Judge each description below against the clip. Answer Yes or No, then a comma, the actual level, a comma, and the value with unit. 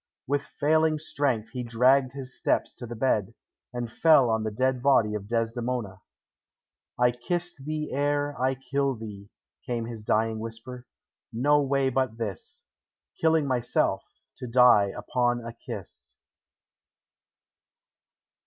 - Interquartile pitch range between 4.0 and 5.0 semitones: No, average, 3.4 semitones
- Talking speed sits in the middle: No, slow, 130 wpm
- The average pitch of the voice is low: Yes, low, 125 Hz